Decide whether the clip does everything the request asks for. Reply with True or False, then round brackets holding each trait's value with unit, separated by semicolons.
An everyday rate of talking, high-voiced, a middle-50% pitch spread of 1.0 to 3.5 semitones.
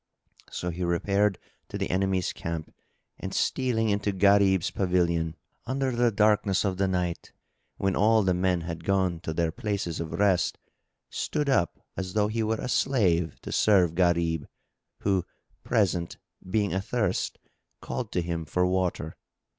False (150 wpm; 95 Hz; 3.2 semitones)